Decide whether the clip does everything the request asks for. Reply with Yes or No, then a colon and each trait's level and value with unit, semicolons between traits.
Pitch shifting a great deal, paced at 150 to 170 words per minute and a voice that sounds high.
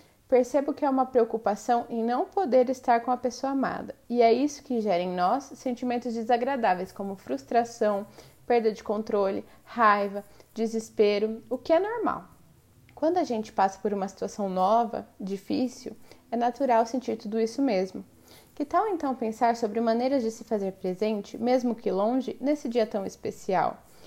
No: average, 3.2 semitones; average, 160 wpm; high, 235 Hz